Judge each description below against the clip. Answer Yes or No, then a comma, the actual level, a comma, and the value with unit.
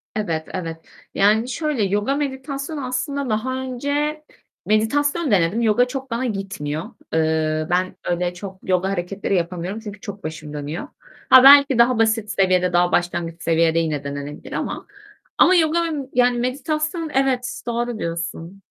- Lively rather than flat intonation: Yes, wide, 7.0 semitones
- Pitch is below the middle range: No, high, 210 Hz